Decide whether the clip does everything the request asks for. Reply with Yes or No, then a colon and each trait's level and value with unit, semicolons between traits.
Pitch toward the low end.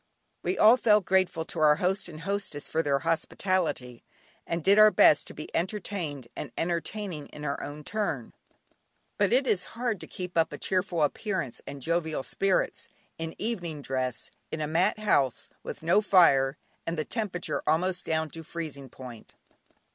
No: medium, 165 Hz